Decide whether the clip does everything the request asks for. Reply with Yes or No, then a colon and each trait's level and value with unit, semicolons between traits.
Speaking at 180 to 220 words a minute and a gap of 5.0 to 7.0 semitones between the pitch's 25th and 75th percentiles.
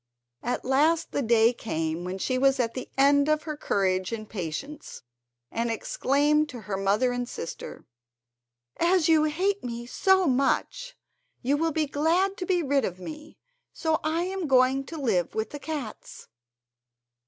No: average, 165 wpm; wide, 5.4 semitones